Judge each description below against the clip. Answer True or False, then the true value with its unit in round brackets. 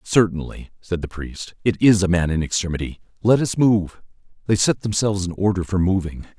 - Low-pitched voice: True (95 Hz)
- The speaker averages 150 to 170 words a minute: False (180 wpm)